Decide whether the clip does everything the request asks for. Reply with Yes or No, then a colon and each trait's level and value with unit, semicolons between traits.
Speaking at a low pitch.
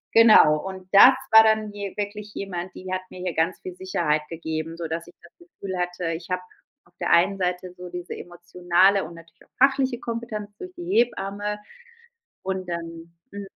No: medium, 185 Hz